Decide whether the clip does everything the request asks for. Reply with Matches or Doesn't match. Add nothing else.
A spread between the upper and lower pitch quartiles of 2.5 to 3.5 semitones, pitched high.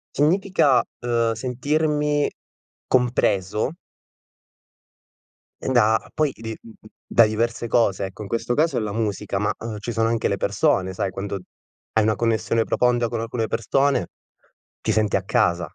Doesn't match